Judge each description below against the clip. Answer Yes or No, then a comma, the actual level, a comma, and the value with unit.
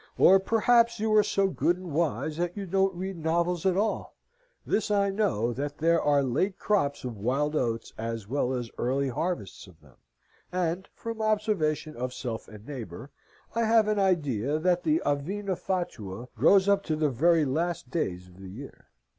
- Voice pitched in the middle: Yes, medium, 160 Hz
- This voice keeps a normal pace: Yes, average, 180 wpm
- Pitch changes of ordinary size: No, wide, 7.3 semitones